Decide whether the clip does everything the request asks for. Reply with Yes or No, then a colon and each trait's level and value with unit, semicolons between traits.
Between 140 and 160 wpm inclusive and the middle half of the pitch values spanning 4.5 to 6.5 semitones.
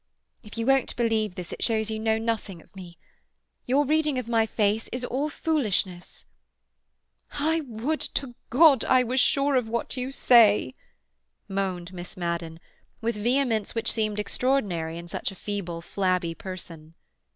Yes: average, 155 wpm; wide, 5.5 semitones